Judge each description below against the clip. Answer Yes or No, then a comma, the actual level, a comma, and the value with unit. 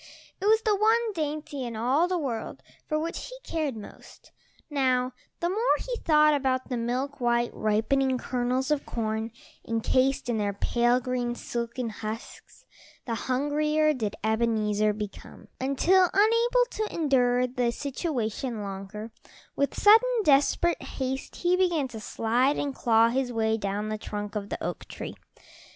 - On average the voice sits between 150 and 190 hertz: No, very high, 255 Hz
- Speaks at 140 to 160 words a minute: Yes, average, 150 wpm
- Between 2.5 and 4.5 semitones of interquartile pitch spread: No, average, 5.2 semitones